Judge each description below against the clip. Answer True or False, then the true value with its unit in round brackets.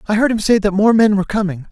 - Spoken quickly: True (315 wpm)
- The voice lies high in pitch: True (205 Hz)